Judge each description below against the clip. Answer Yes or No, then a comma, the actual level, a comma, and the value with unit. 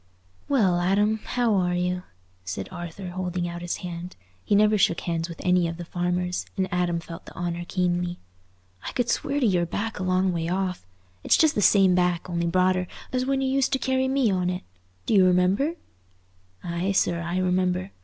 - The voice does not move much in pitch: Yes, narrow, 2.3 semitones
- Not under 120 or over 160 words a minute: No, average, 195 wpm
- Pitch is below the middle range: No, medium, 180 Hz